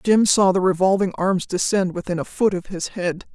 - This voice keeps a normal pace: No, fast, 215 wpm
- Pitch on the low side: No, high, 190 Hz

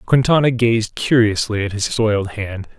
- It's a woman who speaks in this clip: No, male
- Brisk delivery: No, average, 150 wpm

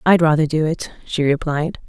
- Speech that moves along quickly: No, average, 190 wpm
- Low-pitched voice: No, medium, 155 Hz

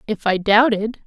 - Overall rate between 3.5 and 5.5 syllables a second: Yes, 4.7 syllables/s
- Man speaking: No, female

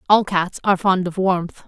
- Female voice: Yes, female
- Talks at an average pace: No, fast, 215 wpm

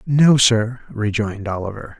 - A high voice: No, low, 115 Hz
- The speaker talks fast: No, slow, 120 wpm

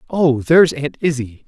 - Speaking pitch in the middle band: Yes, medium, 145 Hz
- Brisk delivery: No, average, 165 wpm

